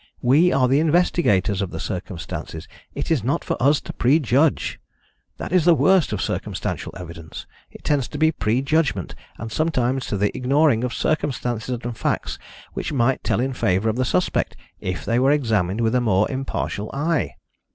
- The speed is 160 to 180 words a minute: Yes, average, 170 wpm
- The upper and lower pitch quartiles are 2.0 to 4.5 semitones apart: No, wide, 5.5 semitones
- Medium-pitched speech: No, low, 125 Hz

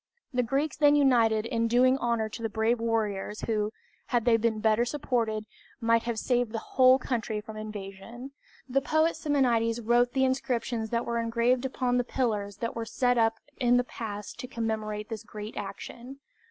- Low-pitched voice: No, high, 230 Hz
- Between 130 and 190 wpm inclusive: Yes, average, 180 wpm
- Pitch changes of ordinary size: No, narrow, 2.2 semitones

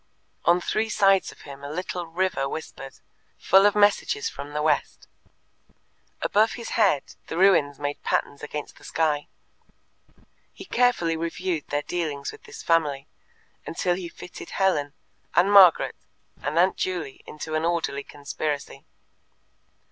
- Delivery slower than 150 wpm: Yes, average, 140 wpm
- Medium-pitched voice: Yes, medium, 165 Hz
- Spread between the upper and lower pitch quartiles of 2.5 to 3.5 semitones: No, average, 4.5 semitones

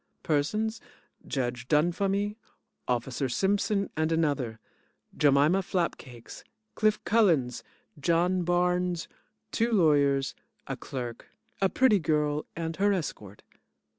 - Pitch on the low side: No, medium, 165 Hz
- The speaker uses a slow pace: Yes, slow, 100 wpm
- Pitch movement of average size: No, wide, 5.7 semitones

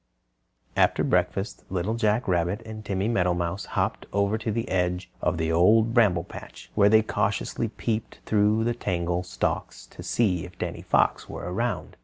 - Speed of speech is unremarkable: Yes, average, 165 wpm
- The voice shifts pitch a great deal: No, average, 3.6 semitones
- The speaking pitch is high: No, low, 100 Hz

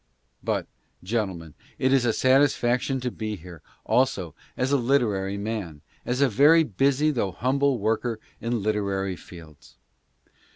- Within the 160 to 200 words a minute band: No, slow, 135 wpm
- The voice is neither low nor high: No, low, 115 Hz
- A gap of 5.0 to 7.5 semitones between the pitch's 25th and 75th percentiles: Yes, average, 5.3 semitones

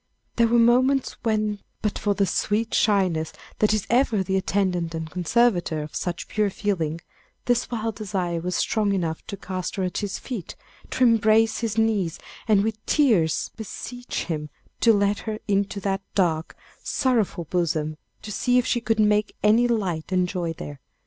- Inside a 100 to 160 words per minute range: No, average, 170 wpm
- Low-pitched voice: No, high, 205 Hz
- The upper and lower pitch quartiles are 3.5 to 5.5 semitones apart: Yes, average, 4.0 semitones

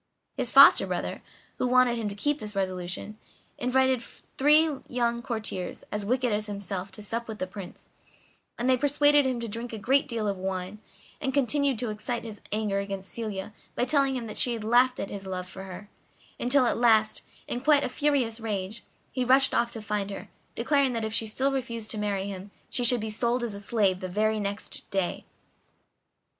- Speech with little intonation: No, average, 3.8 semitones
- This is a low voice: No, high, 225 Hz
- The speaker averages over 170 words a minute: Yes, average, 200 wpm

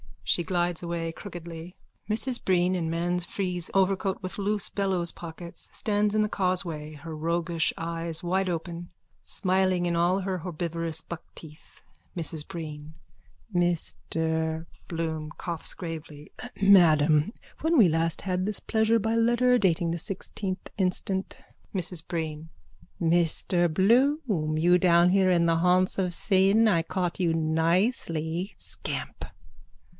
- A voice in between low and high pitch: Yes, medium, 175 Hz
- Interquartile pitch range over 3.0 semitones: No, narrow, 2.6 semitones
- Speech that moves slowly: Yes, slow, 130 wpm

